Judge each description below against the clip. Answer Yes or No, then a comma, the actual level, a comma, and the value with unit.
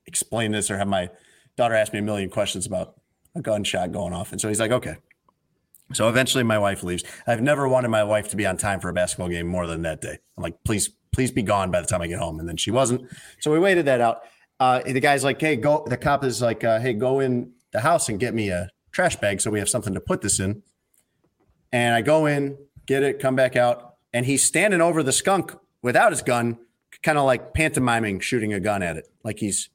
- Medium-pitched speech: No, low, 120 Hz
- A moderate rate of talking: No, fast, 250 wpm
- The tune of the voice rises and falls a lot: No, average, 4.4 semitones